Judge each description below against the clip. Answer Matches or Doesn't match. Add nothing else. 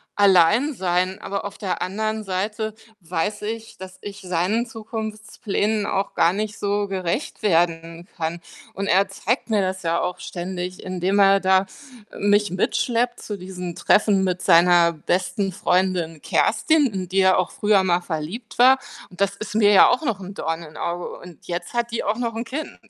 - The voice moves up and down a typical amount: Matches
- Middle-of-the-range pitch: Doesn't match